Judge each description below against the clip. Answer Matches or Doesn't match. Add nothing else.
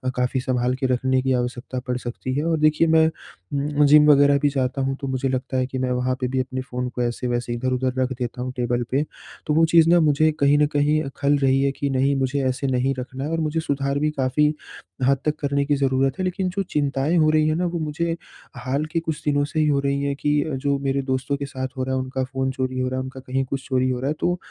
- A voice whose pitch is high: Doesn't match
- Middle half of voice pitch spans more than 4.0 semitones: Doesn't match